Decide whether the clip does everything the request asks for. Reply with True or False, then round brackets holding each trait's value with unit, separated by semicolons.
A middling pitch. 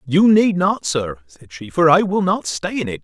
True (160 Hz)